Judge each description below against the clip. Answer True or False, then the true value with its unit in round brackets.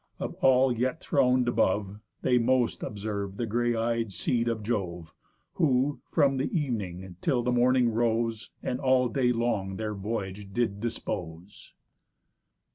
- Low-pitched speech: True (115 Hz)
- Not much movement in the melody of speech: False (3.7 semitones)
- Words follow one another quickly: False (140 wpm)